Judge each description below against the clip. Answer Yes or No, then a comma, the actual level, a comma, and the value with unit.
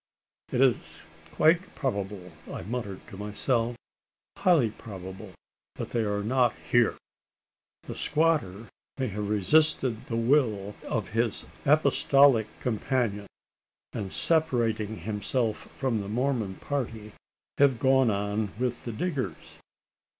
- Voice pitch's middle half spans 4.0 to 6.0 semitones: Yes, average, 4.3 semitones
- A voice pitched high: No, low, 115 Hz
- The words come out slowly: Yes, slow, 115 wpm